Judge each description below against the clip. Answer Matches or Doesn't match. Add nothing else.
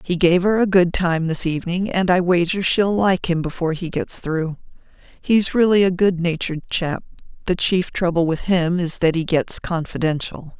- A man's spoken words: Doesn't match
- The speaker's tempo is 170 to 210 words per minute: Matches